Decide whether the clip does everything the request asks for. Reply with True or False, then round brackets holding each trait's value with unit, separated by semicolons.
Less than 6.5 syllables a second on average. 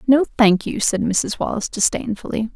True (5.3 syllables/s)